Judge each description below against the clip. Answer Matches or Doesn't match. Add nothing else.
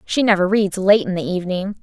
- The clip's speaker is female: Matches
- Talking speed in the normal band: Doesn't match